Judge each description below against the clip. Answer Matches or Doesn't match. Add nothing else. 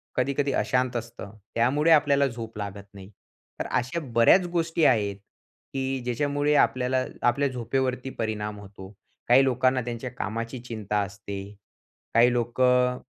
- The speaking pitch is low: Matches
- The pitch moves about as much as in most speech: Matches